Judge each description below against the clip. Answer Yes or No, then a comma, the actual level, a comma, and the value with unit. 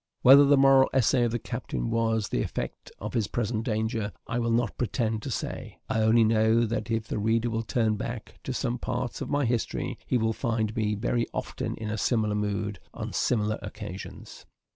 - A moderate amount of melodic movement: No, narrow, 1.9 semitones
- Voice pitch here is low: Yes, low, 115 Hz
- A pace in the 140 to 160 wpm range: No, average, 200 wpm